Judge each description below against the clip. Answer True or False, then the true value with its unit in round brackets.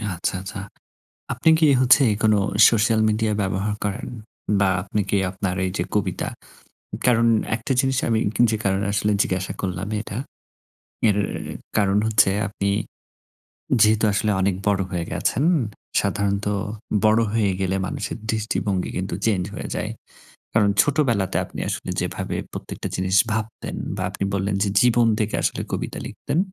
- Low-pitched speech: True (105 Hz)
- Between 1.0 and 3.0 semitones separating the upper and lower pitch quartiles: True (2.5 semitones)